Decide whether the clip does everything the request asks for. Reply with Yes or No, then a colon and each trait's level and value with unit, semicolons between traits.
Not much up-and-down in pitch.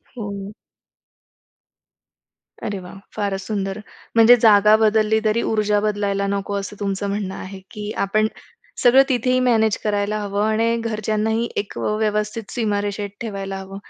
Yes: narrow, 1.6 semitones